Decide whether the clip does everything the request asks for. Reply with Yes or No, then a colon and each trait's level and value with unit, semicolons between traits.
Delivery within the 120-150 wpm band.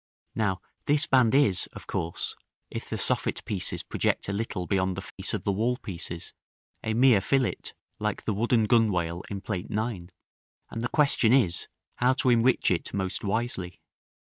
No: average, 165 wpm